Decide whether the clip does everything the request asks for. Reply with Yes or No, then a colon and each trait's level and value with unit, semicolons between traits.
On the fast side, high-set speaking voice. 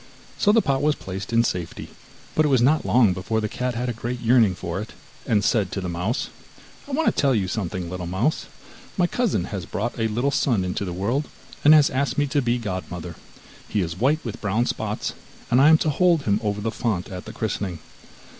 No: fast, 225 wpm; low, 115 Hz